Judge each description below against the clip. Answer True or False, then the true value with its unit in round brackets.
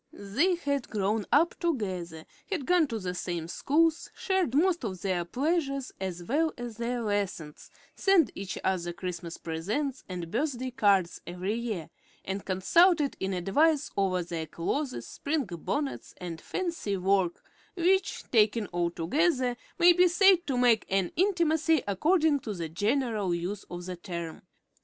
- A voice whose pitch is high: True (220 Hz)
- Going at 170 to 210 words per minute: False (150 wpm)